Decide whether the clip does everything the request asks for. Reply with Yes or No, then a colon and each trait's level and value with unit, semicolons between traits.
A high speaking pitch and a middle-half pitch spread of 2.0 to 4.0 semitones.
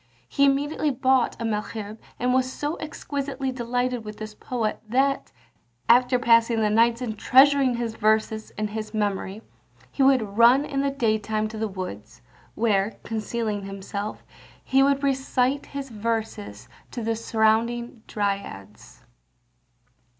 Yes: high, 230 Hz; average, 3.4 semitones